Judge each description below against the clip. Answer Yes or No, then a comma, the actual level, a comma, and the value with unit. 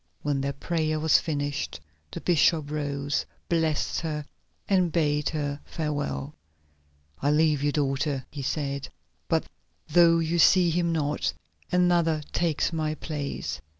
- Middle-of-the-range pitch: Yes, medium, 150 Hz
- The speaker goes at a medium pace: No, slow, 130 wpm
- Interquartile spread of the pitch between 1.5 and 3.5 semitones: Yes, narrow, 2.4 semitones